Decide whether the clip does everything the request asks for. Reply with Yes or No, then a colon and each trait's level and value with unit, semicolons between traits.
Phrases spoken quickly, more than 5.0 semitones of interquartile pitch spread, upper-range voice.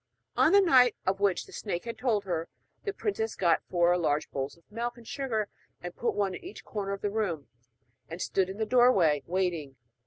Yes: fast, 210 wpm; wide, 5.4 semitones; high, 200 Hz